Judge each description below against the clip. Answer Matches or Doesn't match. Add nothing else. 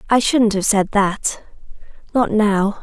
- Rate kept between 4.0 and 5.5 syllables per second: Doesn't match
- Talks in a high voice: Matches